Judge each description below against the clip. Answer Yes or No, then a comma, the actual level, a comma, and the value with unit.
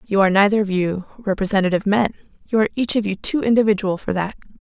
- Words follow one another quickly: Yes, fast, 210 wpm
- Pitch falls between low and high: No, high, 200 Hz